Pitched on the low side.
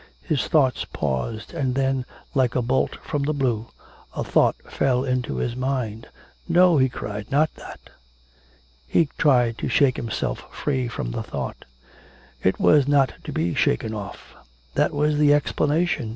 Yes: low, 130 Hz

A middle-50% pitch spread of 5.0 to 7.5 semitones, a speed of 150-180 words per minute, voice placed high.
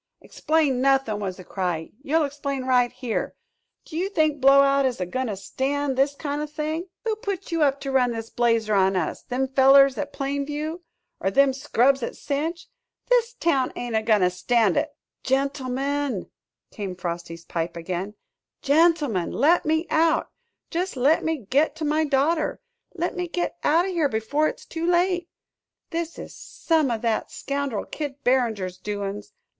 Yes: wide, 5.5 semitones; average, 170 wpm; very high, 275 Hz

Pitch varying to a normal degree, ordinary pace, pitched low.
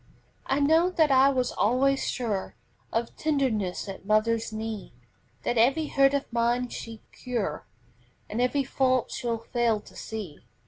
No: average, 3.7 semitones; average, 145 wpm; high, 240 Hz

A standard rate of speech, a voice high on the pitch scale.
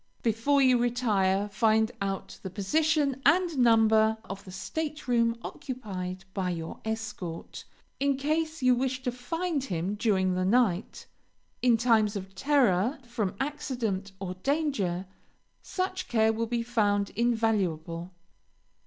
No: slow, 125 wpm; high, 225 Hz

